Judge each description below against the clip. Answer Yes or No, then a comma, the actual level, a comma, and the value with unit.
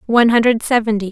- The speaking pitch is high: Yes, high, 225 Hz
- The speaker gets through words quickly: No, average, 160 wpm